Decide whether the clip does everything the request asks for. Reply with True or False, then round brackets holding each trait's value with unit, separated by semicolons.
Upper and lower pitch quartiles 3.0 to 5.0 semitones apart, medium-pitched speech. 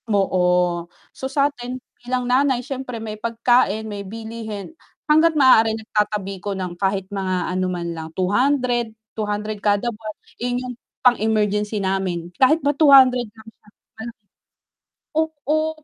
False (3.9 semitones; 220 Hz)